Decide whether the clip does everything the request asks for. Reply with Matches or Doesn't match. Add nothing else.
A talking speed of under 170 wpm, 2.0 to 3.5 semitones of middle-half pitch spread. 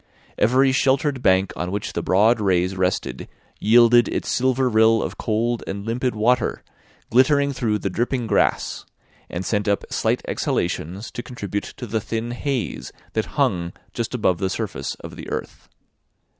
Doesn't match